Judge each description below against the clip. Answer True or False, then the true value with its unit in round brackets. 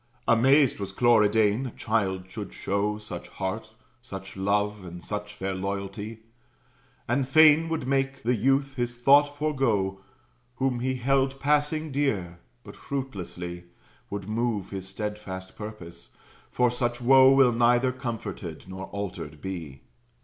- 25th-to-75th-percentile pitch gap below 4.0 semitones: False (5.4 semitones)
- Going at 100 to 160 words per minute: True (135 wpm)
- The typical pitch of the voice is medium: False (110 Hz)